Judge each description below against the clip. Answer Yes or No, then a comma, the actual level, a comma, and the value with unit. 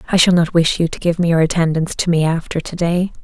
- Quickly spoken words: Yes, fast, 260 wpm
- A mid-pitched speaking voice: Yes, medium, 170 Hz